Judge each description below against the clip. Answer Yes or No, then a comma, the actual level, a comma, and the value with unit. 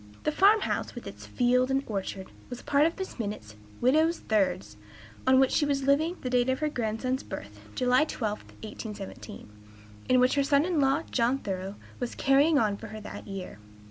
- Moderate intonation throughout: Yes, average, 4.8 semitones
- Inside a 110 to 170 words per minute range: No, average, 200 wpm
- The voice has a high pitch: Yes, very high, 255 Hz